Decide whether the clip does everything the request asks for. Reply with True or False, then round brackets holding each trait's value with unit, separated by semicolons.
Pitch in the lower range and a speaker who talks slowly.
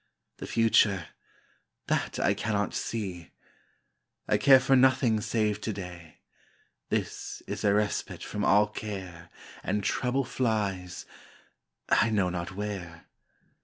True (105 Hz; 120 wpm)